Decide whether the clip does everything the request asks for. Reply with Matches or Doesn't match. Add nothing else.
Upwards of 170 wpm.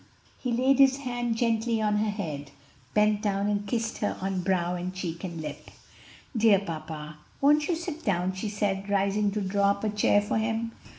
Matches